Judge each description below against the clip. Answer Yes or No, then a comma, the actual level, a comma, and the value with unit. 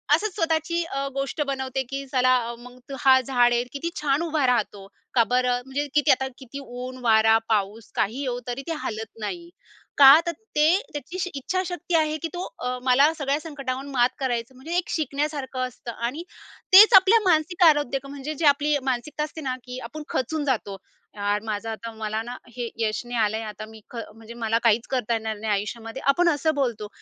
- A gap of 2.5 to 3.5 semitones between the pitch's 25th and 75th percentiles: No, average, 4.3 semitones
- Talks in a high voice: Yes, very high, 265 Hz